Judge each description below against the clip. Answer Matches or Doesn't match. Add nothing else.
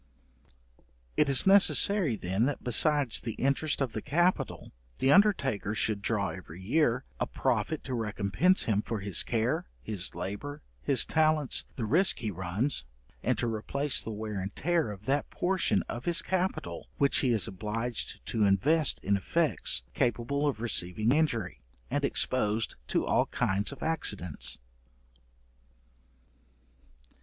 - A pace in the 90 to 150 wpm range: Matches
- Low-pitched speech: Matches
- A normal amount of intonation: Doesn't match